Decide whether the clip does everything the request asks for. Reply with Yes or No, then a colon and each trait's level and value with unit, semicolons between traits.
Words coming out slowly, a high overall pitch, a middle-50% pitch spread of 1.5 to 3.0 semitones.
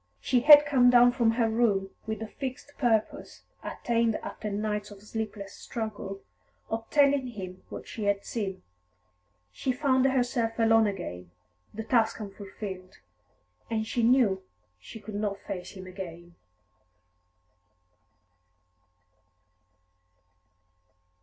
No: slow, 120 wpm; high, 220 Hz; average, 3.5 semitones